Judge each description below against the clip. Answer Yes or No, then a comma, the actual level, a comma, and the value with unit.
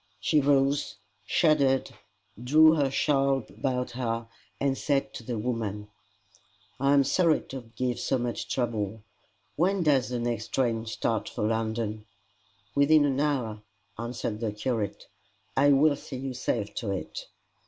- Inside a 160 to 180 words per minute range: No, average, 145 wpm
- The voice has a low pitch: Yes, low, 125 Hz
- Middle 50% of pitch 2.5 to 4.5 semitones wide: Yes, average, 3.7 semitones